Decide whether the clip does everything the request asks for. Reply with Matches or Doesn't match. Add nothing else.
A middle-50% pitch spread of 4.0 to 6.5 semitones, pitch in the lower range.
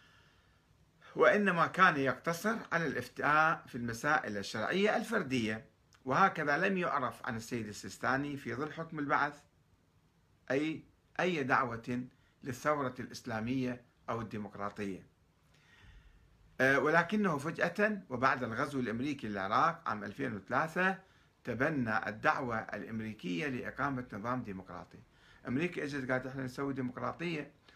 Matches